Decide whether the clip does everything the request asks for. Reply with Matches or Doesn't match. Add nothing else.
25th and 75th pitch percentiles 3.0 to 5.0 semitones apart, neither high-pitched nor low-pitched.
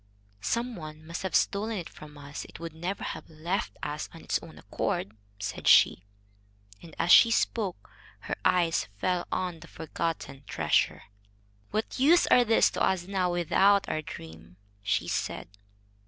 Matches